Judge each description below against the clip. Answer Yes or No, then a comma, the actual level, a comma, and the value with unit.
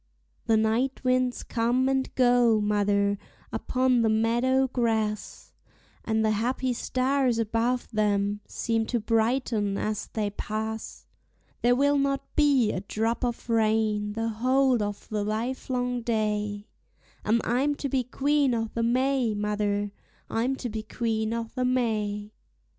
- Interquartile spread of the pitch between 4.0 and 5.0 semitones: No, average, 2.9 semitones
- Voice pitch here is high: Yes, high, 230 Hz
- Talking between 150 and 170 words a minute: No, slow, 135 wpm